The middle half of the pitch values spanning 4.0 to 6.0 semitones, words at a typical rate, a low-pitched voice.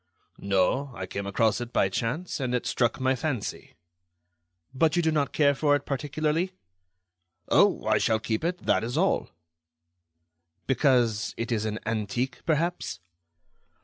Yes: average, 5.2 semitones; average, 145 wpm; low, 130 Hz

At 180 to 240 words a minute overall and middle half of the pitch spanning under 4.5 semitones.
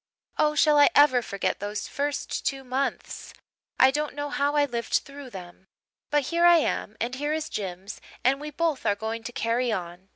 No: average, 195 wpm; average, 5.0 semitones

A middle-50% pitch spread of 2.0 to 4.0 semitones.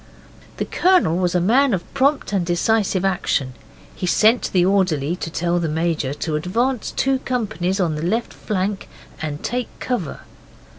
No: average, 5.2 semitones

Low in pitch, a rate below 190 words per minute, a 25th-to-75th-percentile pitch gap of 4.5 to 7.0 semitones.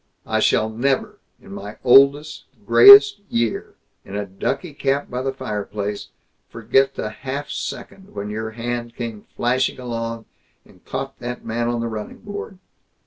No: low, 120 Hz; average, 150 wpm; average, 3.6 semitones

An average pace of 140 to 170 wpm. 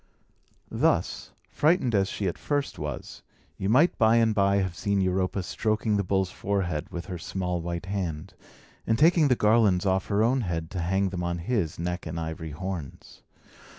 No: average, 180 wpm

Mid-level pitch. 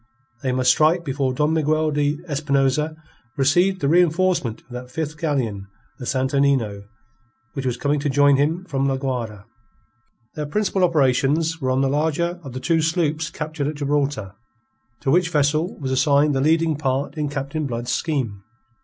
Yes: medium, 145 Hz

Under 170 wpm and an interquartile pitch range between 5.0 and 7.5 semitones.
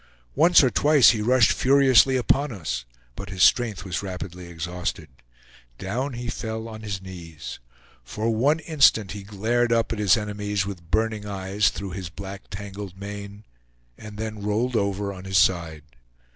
No: average, 160 wpm; average, 3.3 semitones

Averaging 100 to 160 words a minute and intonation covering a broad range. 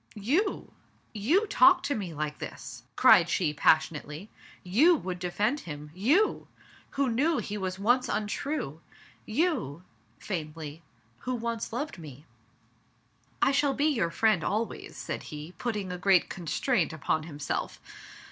Yes: average, 145 wpm; wide, 8.7 semitones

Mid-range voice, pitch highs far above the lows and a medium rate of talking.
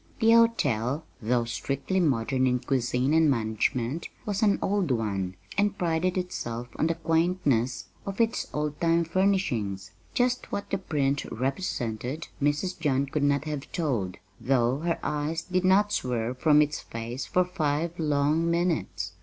Yes: medium, 150 Hz; wide, 5.9 semitones; average, 150 wpm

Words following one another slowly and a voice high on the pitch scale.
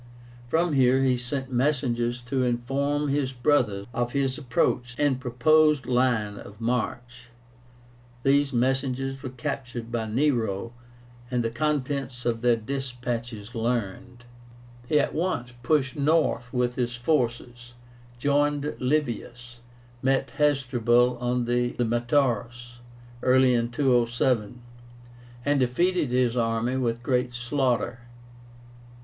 No: slow, 115 wpm; low, 125 Hz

